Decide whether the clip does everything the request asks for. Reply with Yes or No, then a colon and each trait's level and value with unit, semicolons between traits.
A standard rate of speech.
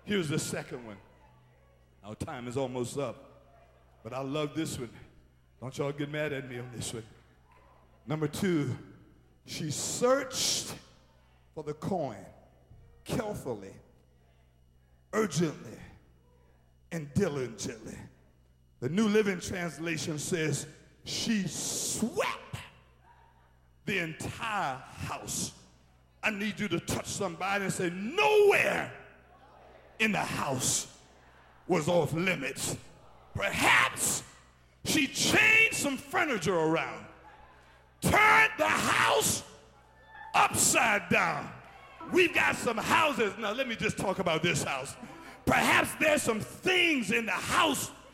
No: slow, 110 wpm